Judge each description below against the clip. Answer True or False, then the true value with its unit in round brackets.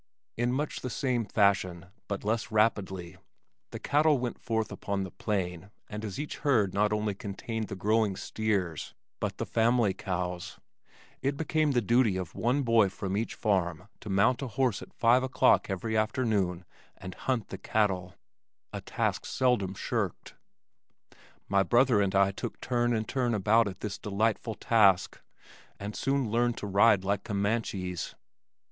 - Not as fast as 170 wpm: True (160 wpm)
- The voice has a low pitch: True (105 Hz)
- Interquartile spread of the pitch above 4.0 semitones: False (3.6 semitones)